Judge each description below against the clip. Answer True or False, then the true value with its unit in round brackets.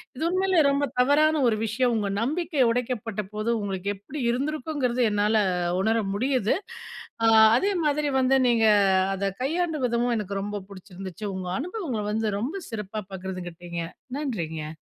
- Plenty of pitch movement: True (5.9 semitones)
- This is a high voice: True (230 Hz)